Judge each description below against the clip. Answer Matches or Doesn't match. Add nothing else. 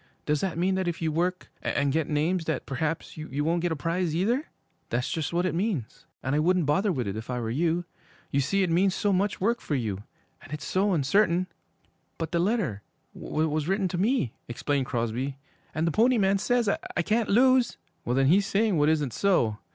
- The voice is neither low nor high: Matches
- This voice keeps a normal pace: Doesn't match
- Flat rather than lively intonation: Doesn't match